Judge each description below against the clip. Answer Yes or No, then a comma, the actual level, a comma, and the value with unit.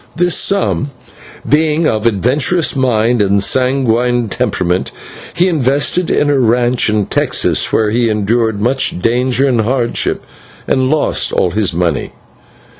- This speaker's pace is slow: Yes, slow, 130 wpm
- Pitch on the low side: Yes, low, 120 Hz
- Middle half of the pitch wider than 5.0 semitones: No, average, 4.1 semitones